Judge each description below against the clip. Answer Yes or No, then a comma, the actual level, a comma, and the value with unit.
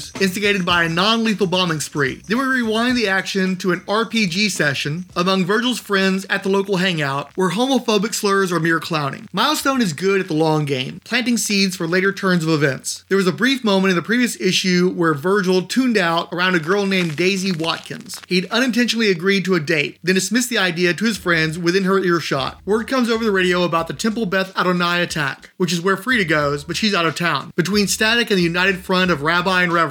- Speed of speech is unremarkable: No, fast, 220 wpm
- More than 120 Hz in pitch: Yes, high, 190 Hz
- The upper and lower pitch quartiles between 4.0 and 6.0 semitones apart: No, average, 3.4 semitones